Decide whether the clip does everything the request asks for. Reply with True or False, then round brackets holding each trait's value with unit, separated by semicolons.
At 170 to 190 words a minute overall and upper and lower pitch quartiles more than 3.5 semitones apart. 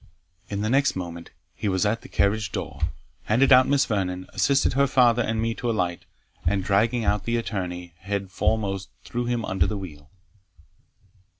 True (175 wpm; 4.0 semitones)